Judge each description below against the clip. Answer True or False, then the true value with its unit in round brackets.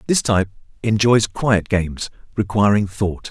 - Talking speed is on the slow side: True (125 wpm)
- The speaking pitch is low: True (105 Hz)